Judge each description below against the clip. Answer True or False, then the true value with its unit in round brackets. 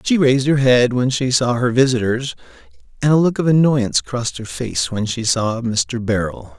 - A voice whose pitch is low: True (125 Hz)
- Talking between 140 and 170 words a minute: False (200 wpm)